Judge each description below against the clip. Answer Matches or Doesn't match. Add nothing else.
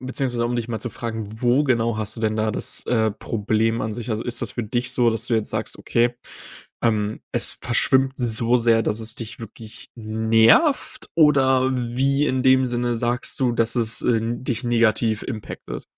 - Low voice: Matches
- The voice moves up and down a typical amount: Doesn't match